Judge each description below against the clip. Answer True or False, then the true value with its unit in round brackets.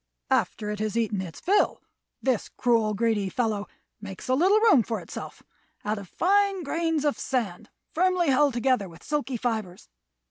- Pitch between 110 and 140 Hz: False (240 Hz)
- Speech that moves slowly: False (155 wpm)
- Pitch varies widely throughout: True (6.4 semitones)